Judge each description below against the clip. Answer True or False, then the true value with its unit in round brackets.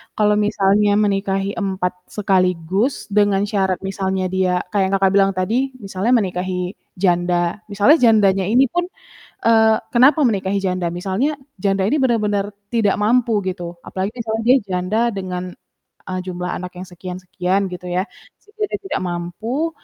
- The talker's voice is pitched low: False (195 Hz)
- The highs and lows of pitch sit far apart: False (3.0 semitones)